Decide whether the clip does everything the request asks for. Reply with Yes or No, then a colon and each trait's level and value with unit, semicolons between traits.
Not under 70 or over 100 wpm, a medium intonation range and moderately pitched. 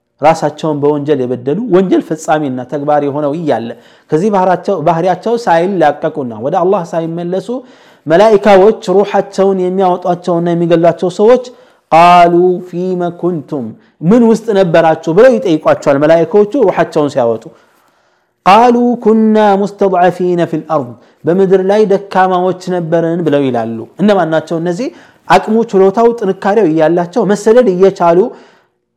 Yes: average, 95 wpm; average, 4.0 semitones; medium, 175 Hz